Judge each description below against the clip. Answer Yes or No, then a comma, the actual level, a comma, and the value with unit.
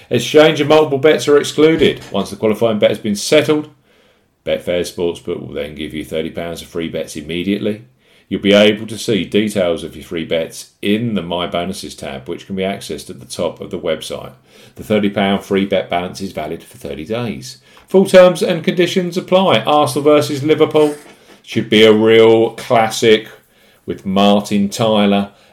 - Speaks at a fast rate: No, average, 175 wpm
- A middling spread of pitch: No, wide, 7.7 semitones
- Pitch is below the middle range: Yes, low, 105 Hz